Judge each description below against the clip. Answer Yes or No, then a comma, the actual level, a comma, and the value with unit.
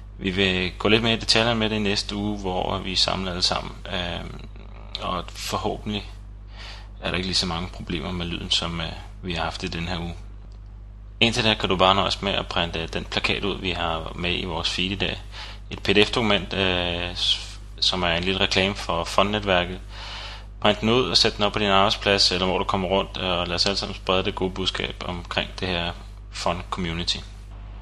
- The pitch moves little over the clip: Yes, narrow, 1.9 semitones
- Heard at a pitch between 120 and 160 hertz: No, low, 100 Hz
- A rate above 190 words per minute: Yes, average, 205 wpm